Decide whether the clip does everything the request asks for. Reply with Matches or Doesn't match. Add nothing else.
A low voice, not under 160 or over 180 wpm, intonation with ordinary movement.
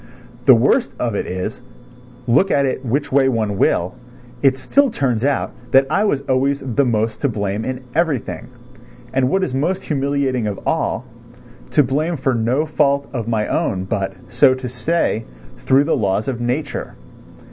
Matches